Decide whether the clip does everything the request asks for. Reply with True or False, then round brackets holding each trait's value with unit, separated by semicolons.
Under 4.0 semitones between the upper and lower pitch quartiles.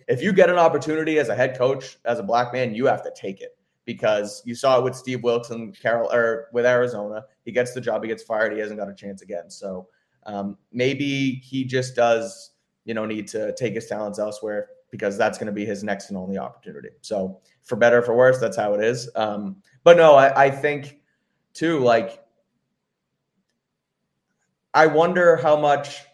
False (5.0 semitones)